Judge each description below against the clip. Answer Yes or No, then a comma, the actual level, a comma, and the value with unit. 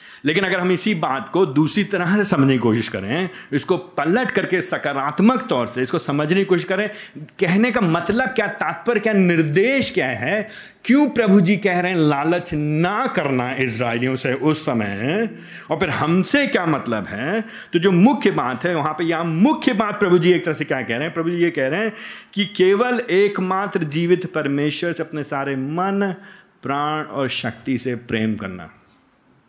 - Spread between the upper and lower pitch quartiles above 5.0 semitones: Yes, wide, 5.6 semitones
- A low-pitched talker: No, medium, 175 Hz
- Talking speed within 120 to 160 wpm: No, average, 185 wpm